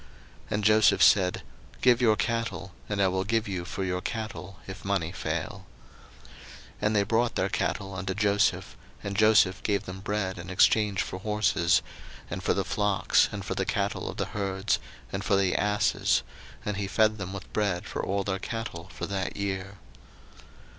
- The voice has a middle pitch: No, low, 100 Hz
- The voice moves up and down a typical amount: No, narrow, 2.0 semitones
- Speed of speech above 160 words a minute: Yes, average, 180 wpm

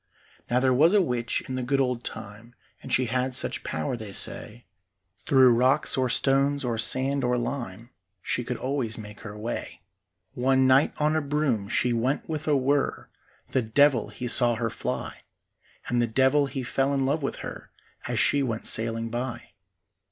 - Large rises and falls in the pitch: No, average, 2.8 semitones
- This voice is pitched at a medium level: No, low, 125 Hz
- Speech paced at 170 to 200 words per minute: Yes, average, 180 wpm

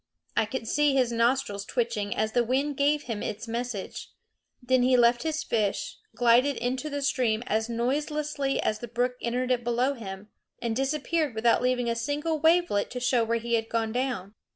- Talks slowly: No, average, 185 wpm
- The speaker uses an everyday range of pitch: Yes, average, 3.0 semitones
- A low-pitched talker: No, high, 245 Hz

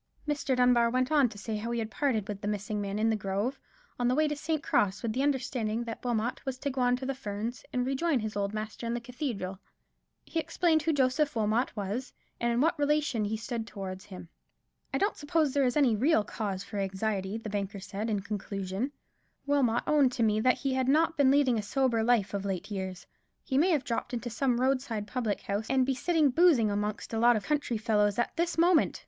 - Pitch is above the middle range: Yes, high, 235 Hz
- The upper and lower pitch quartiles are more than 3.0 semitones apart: Yes, average, 4.5 semitones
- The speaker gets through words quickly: Yes, fast, 225 wpm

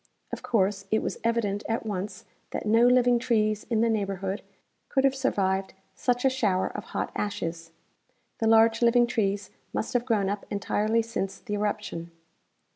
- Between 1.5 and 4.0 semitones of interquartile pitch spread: Yes, average, 2.9 semitones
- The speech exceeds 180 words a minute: No, average, 170 wpm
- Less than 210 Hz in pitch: No, high, 215 Hz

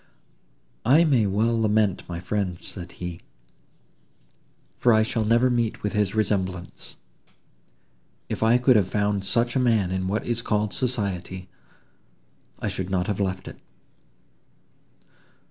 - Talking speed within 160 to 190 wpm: No, slow, 135 wpm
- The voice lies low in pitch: Yes, low, 105 Hz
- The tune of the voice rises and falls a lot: No, average, 3.6 semitones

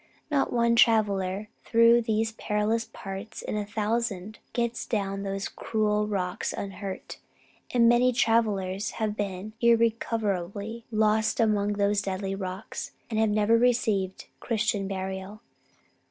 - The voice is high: Yes, high, 210 Hz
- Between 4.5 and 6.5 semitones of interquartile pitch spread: No, narrow, 2.6 semitones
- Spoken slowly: Yes, slow, 125 wpm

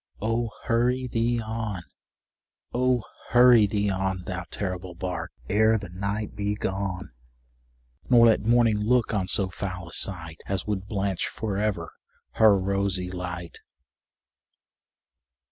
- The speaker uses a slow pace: Yes, slow, 130 wpm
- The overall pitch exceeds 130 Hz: No, low, 100 Hz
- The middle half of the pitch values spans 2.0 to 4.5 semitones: Yes, average, 3.3 semitones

